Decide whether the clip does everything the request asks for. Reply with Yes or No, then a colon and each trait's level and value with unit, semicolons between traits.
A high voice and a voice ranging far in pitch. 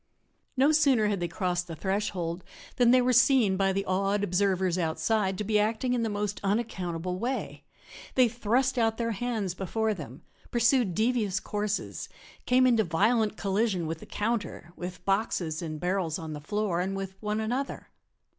No: high, 205 Hz; average, 4.2 semitones